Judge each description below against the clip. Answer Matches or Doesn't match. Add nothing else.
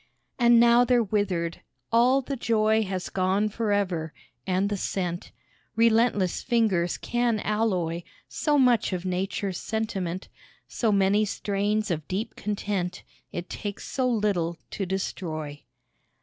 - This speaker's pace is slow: Matches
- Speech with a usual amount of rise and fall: Matches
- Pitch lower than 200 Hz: Doesn't match